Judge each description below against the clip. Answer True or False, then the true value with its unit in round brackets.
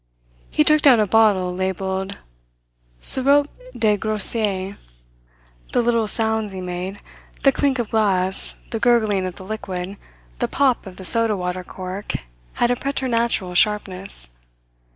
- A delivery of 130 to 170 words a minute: True (135 wpm)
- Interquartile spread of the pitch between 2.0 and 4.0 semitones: True (3.7 semitones)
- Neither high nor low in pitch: False (210 Hz)